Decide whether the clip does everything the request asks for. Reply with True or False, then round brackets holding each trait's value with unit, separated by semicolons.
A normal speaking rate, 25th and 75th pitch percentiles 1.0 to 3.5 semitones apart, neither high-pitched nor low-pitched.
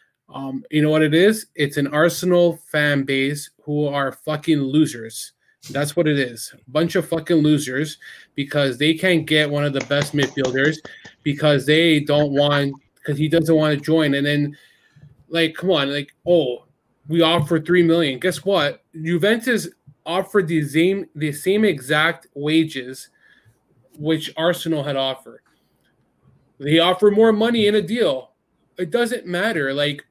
True (155 wpm; 3.1 semitones; 155 Hz)